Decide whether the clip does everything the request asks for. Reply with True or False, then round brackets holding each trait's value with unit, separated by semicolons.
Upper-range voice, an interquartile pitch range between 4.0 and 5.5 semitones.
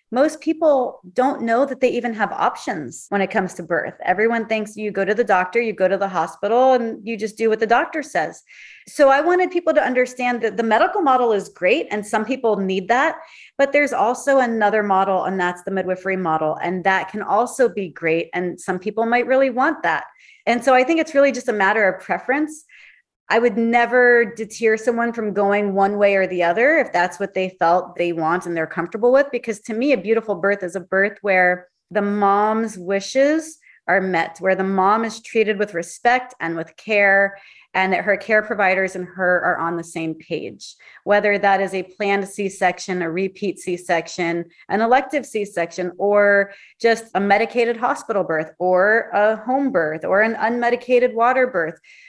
True (210 Hz; 4.5 semitones)